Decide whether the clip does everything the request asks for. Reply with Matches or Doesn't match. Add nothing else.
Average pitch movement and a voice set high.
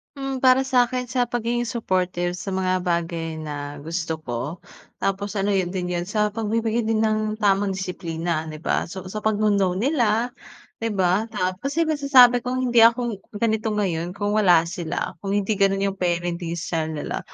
Matches